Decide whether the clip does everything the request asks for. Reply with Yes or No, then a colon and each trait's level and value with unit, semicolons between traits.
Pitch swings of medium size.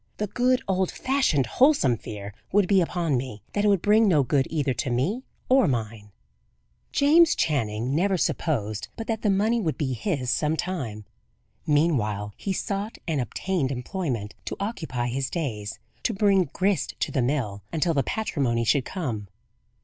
No: wide, 8.3 semitones